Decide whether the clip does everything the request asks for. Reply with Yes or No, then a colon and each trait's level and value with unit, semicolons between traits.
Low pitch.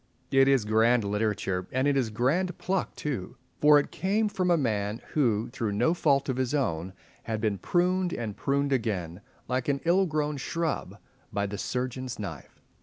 Yes: low, 130 Hz